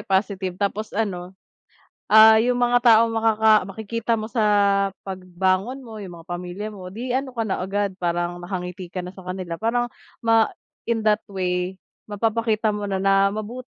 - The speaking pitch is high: Yes, high, 205 Hz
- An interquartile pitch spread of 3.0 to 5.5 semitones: Yes, average, 3.3 semitones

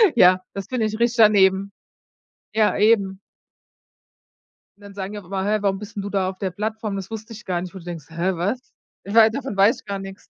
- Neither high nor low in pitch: No, high, 200 Hz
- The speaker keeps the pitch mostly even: Yes, narrow, 2.2 semitones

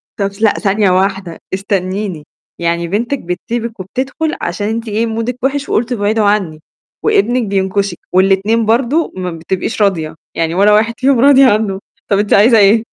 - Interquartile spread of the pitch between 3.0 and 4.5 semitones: Yes, average, 3.4 semitones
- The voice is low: No, high, 205 Hz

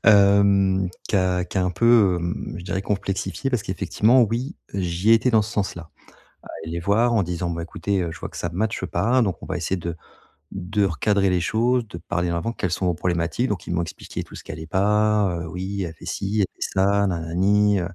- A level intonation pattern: No, average, 3.1 semitones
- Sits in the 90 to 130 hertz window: Yes, very low, 95 Hz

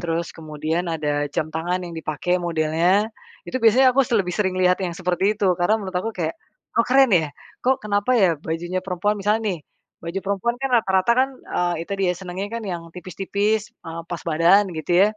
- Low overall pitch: No, medium, 185 Hz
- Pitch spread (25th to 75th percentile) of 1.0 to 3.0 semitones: No, average, 3.7 semitones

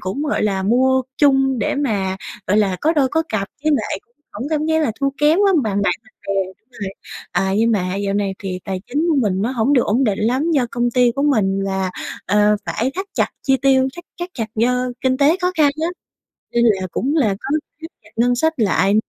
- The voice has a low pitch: No, high, 245 Hz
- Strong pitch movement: Yes, wide, 5.8 semitones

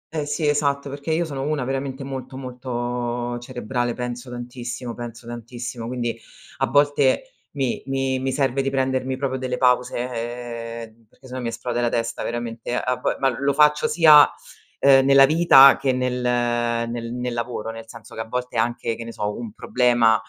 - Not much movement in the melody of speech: Yes, narrow, 2.1 semitones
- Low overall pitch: Yes, low, 125 Hz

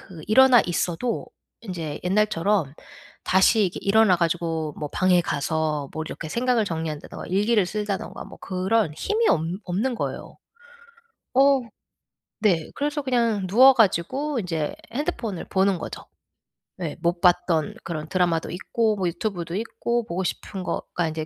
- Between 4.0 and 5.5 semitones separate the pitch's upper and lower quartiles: Yes, average, 5.2 semitones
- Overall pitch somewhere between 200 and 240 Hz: No, medium, 185 Hz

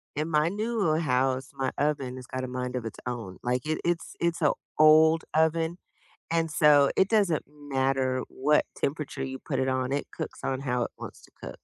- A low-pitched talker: No, medium, 145 Hz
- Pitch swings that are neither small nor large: Yes, average, 3.6 semitones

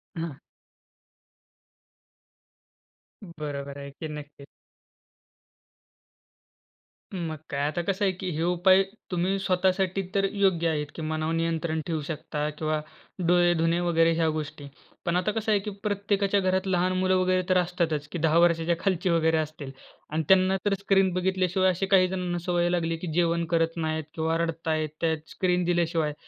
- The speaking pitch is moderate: Yes, medium, 170 Hz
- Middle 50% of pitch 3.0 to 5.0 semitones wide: No, narrow, 2.6 semitones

